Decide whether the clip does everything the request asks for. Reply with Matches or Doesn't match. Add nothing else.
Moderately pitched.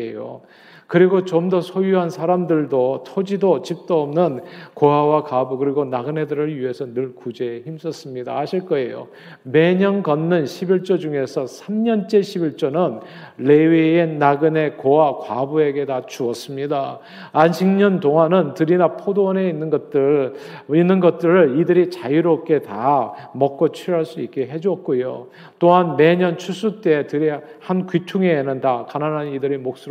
Matches